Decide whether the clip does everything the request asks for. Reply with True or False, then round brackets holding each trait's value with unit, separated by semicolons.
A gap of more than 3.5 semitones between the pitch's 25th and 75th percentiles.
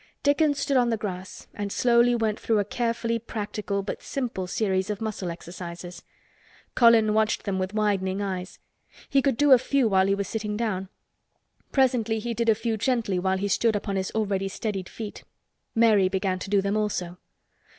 False (3.2 semitones)